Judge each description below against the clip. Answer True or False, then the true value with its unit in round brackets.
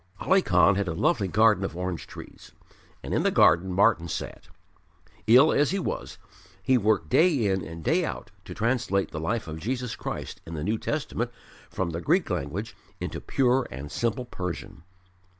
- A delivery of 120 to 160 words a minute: False (180 wpm)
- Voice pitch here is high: False (100 Hz)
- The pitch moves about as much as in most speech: False (6.3 semitones)